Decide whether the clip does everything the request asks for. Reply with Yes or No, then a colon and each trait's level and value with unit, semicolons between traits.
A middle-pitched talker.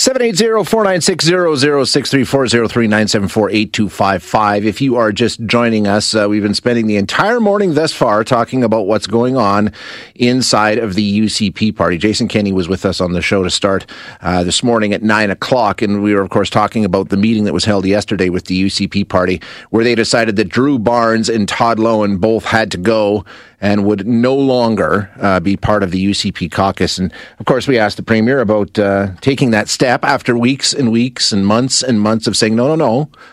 No: low, 110 Hz